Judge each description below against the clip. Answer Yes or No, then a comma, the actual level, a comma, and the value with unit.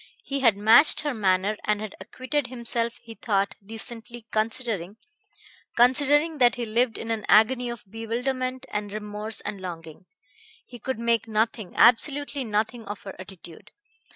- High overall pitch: Yes, high, 225 Hz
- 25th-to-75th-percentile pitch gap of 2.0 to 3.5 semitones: Yes, average, 3.1 semitones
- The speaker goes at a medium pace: Yes, average, 150 wpm